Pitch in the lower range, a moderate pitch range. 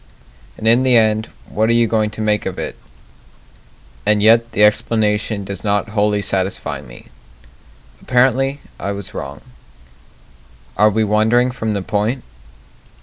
No: low, 110 Hz; narrow, 2.0 semitones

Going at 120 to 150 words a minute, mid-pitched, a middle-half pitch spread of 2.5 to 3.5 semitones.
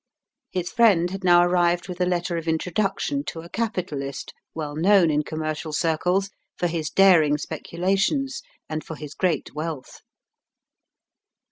Yes: average, 140 wpm; medium, 175 Hz; average, 3.2 semitones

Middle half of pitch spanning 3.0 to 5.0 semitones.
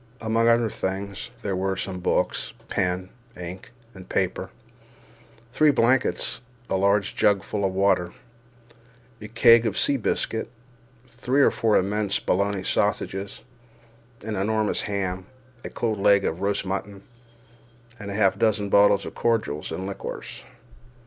No: narrow, 2.4 semitones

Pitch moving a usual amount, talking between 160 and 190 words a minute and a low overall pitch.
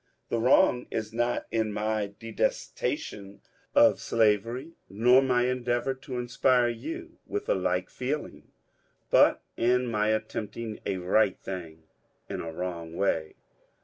No: average, 3.7 semitones; slow, 135 wpm; low, 110 Hz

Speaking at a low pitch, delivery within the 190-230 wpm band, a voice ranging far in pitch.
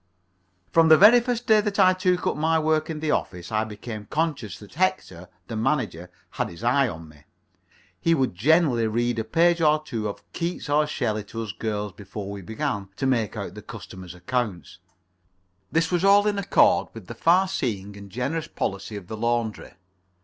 Yes: low, 120 Hz; average, 195 wpm; wide, 7.9 semitones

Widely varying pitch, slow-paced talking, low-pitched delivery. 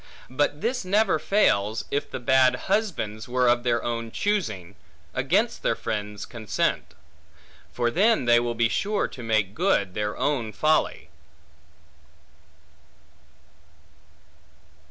Yes: wide, 6.5 semitones; slow, 115 wpm; low, 120 Hz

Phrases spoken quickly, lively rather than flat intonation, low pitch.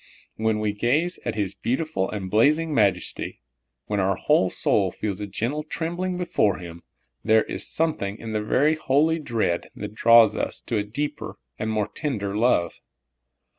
No: average, 175 wpm; wide, 6.5 semitones; low, 110 Hz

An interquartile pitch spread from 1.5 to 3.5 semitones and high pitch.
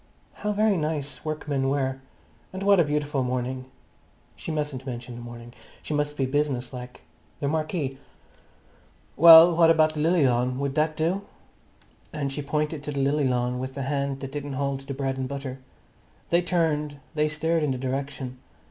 No: narrow, 2.6 semitones; medium, 140 Hz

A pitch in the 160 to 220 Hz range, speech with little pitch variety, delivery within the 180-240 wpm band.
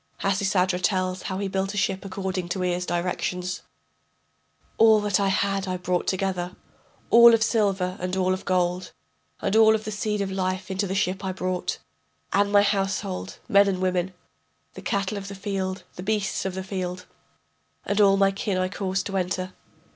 Yes: high, 190 Hz; narrow, 1.4 semitones; average, 185 wpm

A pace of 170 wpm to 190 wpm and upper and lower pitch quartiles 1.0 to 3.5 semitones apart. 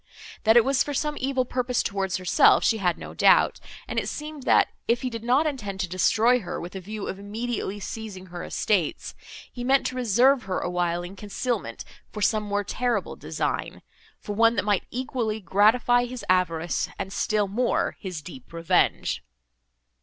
No: average, 185 wpm; average, 4.6 semitones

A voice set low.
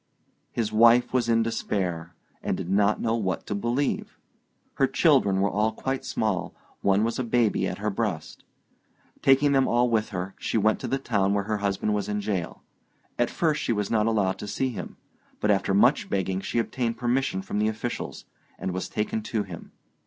Yes: low, 105 Hz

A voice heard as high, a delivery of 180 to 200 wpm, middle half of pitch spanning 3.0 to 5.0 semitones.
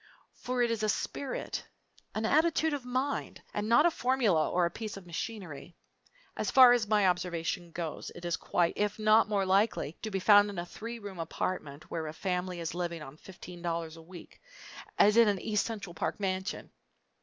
Yes: high, 195 Hz; average, 195 wpm; average, 4.4 semitones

